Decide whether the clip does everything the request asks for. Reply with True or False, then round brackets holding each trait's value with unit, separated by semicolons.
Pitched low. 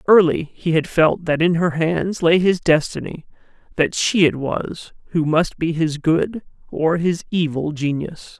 False (165 Hz)